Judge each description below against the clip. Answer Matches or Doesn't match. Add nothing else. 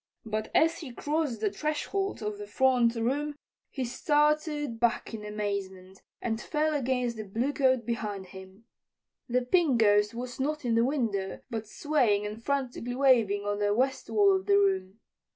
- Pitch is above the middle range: Matches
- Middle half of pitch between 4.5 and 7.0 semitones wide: Matches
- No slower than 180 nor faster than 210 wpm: Doesn't match